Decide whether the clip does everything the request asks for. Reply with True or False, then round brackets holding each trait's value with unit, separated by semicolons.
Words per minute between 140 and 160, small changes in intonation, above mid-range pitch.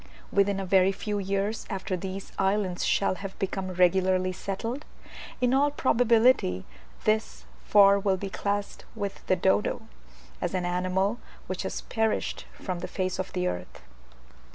True (150 wpm; 2.0 semitones; 195 Hz)